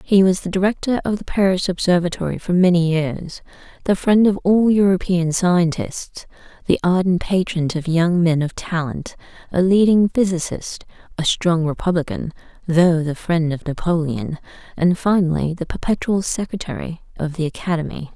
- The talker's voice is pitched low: No, medium, 175 Hz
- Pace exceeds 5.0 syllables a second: No, 4.9 syllables/s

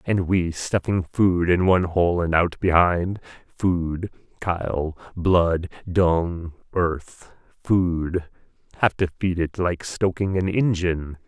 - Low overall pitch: Yes, very low, 90 Hz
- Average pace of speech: No, slow, 130 wpm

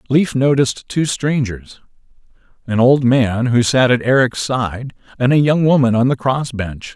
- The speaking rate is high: No, average, 175 wpm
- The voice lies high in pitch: No, low, 125 Hz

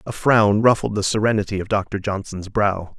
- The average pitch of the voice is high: No, low, 105 Hz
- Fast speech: No, average, 180 wpm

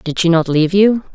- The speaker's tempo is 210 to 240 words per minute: No, fast, 260 wpm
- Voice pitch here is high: No, medium, 180 Hz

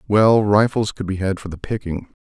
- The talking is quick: Yes, fast, 215 wpm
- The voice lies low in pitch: Yes, low, 100 Hz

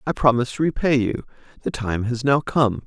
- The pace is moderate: No, fast, 210 wpm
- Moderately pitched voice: No, low, 130 Hz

